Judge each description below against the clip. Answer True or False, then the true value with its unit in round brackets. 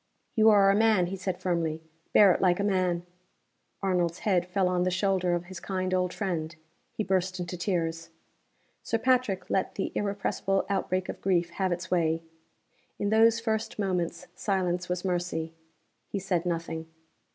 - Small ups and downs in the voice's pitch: True (2.0 semitones)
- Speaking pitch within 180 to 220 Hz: True (185 Hz)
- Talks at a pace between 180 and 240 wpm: False (165 wpm)